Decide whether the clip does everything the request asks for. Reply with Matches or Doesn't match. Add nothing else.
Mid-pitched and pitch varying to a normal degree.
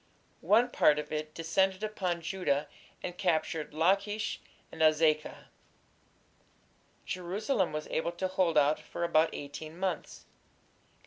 Matches